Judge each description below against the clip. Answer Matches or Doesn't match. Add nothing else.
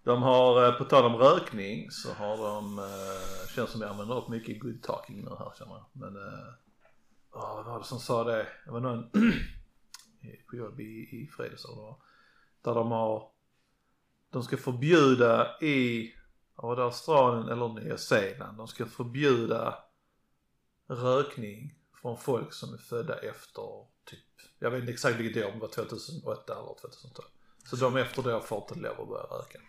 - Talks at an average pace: Matches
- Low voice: Matches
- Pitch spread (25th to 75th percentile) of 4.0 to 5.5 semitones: Matches